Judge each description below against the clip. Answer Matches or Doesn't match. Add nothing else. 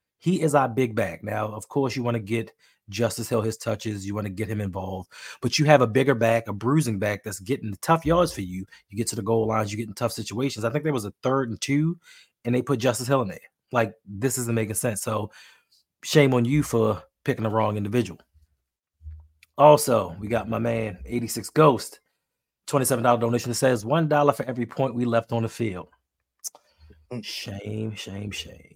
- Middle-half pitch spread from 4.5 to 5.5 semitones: Doesn't match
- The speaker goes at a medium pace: Doesn't match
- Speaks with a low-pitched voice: Matches